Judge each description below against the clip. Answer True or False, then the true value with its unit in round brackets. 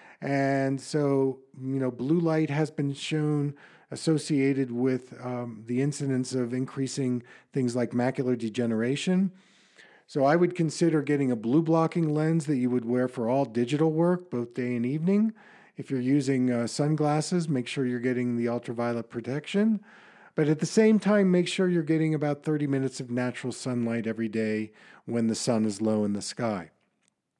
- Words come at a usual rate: True (170 wpm)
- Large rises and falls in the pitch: False (4.2 semitones)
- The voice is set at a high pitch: False (135 Hz)